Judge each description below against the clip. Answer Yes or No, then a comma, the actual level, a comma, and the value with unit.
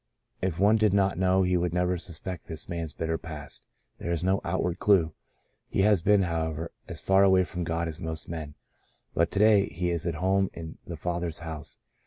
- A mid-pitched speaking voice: No, very low, 85 Hz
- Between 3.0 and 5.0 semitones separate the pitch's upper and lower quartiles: No, narrow, 2.6 semitones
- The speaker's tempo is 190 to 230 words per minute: Yes, fast, 205 wpm